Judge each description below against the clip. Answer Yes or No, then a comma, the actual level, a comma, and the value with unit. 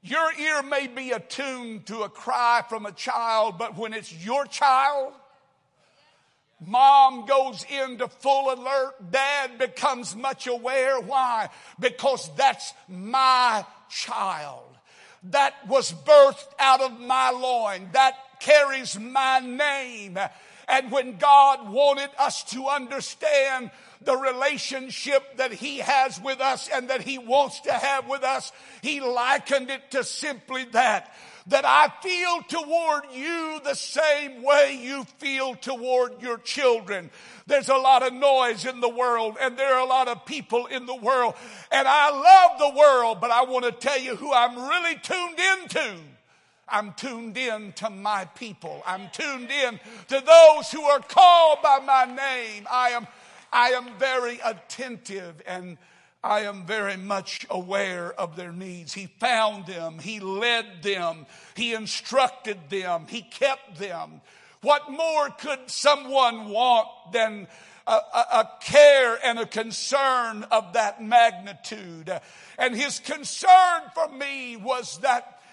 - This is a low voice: No, very high, 260 Hz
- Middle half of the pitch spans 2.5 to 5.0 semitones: Yes, average, 3.5 semitones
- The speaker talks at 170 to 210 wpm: No, average, 145 wpm